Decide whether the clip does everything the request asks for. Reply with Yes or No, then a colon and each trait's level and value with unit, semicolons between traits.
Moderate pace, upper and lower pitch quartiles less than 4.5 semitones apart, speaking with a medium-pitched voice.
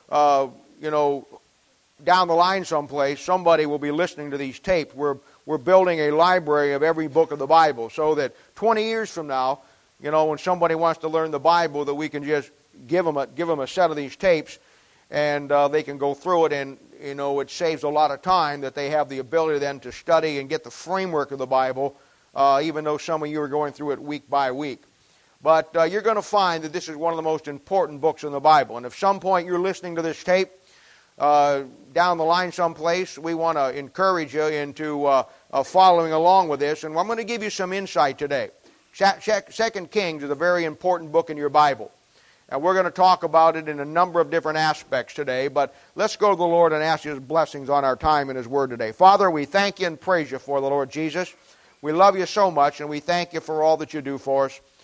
No: fast, 240 wpm; average, 3.6 semitones; medium, 155 Hz